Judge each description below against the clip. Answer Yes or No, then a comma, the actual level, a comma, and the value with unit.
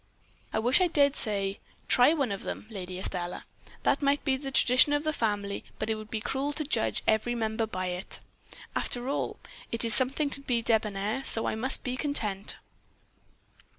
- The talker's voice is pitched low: No, high, 230 Hz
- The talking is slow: No, average, 185 wpm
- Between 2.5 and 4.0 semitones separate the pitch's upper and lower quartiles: No, average, 4.5 semitones